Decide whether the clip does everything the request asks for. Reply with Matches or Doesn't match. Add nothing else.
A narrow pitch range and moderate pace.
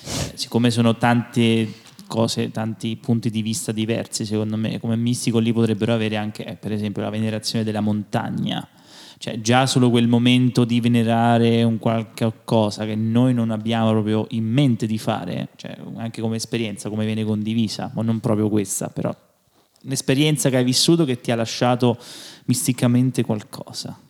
Matches